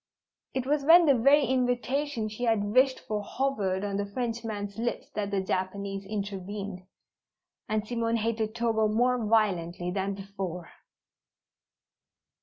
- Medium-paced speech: No, slow, 130 wpm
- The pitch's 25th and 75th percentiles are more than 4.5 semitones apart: No, average, 3.5 semitones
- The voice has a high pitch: Yes, high, 215 Hz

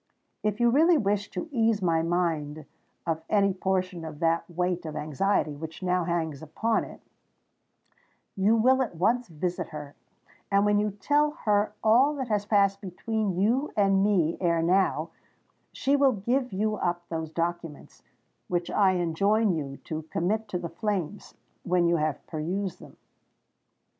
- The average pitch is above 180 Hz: Yes, high, 190 Hz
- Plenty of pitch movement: No, average, 4.2 semitones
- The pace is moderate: Yes, average, 160 wpm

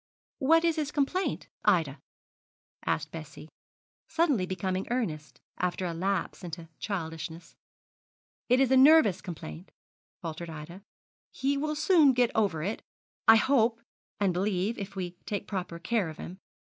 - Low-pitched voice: No, high, 195 Hz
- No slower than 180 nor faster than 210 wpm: No, average, 140 wpm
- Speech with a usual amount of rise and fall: No, wide, 7.2 semitones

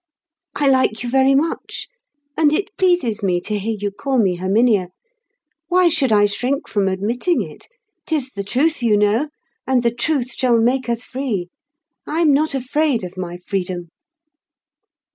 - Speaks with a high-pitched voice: Yes, high, 245 Hz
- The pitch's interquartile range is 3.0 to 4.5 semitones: No, wide, 5.5 semitones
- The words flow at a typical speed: Yes, average, 160 wpm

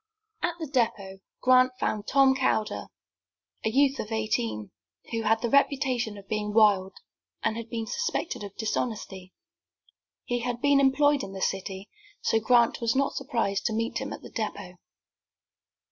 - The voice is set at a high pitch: Yes, high, 225 Hz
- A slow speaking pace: No, average, 160 wpm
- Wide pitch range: No, average, 4.1 semitones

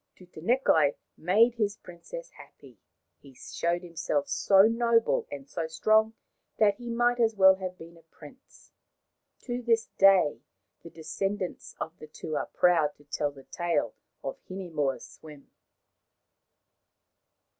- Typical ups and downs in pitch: No, wide, 5.8 semitones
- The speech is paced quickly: No, slow, 135 wpm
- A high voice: No, medium, 180 Hz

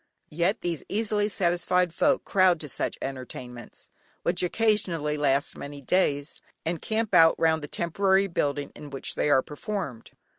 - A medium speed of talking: Yes, average, 150 wpm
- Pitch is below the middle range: No, medium, 165 Hz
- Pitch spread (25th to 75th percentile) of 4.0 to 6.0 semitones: Yes, average, 4.9 semitones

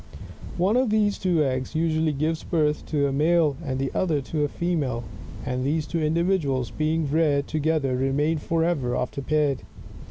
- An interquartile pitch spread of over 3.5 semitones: No, average, 3.1 semitones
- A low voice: No, medium, 155 Hz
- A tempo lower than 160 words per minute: No, average, 165 wpm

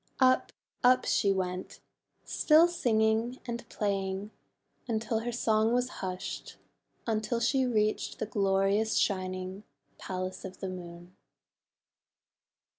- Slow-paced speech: Yes, slow, 115 wpm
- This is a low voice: No, high, 215 Hz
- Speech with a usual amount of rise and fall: Yes, average, 3.8 semitones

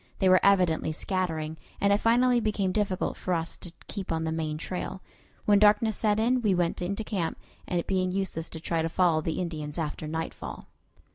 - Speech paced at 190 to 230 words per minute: Yes, average, 195 wpm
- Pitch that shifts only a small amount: No, average, 3.9 semitones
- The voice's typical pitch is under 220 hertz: Yes, medium, 185 Hz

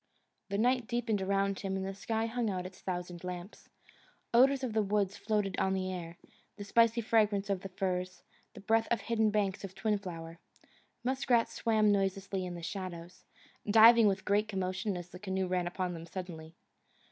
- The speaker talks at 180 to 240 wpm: Yes, average, 185 wpm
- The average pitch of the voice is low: No, high, 195 Hz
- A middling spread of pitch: Yes, average, 3.1 semitones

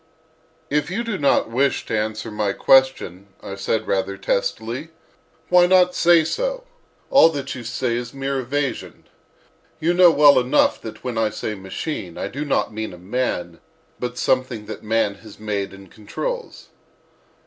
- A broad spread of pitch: Yes, wide, 5.9 semitones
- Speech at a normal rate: Yes, average, 160 wpm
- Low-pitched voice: Yes, low, 125 Hz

